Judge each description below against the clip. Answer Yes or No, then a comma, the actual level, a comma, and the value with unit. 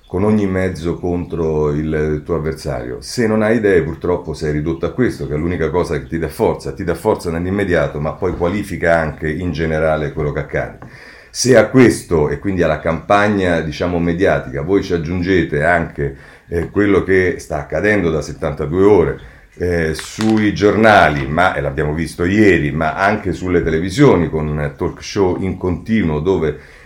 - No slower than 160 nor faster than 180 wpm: Yes, fast, 170 wpm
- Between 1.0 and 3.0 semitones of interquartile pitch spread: No, average, 3.4 semitones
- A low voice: Yes, very low, 85 Hz